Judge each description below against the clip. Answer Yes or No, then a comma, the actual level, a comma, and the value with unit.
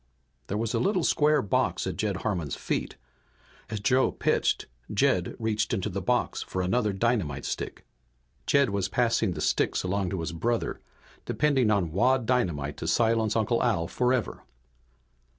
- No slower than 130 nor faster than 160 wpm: Yes, average, 155 wpm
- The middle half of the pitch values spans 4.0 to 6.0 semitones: Yes, average, 4.7 semitones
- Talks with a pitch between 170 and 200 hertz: No, low, 110 Hz